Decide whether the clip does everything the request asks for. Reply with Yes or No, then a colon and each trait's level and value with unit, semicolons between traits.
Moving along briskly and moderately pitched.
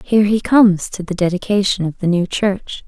No: fast, 210 wpm; high, 195 Hz